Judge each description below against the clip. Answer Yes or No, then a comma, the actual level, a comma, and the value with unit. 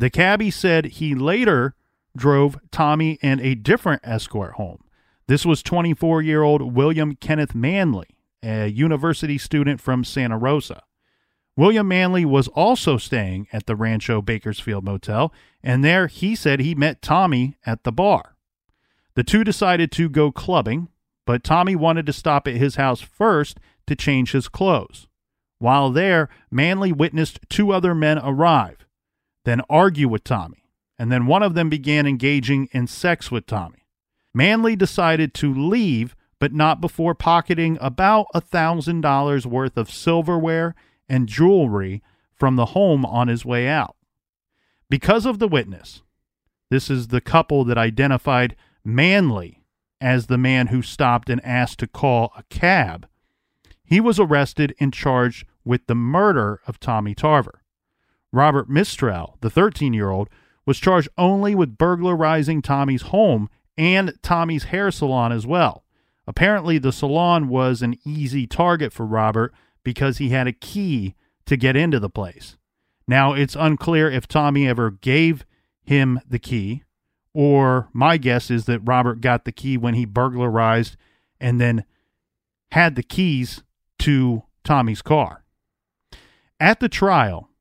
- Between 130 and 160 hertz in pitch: Yes, medium, 140 Hz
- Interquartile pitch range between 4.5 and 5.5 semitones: Yes, average, 5.1 semitones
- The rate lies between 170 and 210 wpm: No, average, 150 wpm